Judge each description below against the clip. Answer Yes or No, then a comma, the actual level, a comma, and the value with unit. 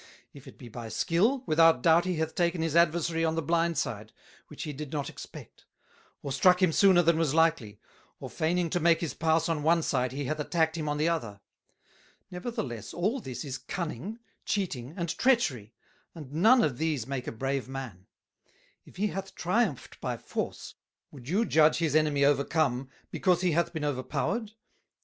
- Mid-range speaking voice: Yes, medium, 160 Hz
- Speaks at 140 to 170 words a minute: No, average, 185 wpm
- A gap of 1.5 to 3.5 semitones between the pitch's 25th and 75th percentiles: No, average, 3.9 semitones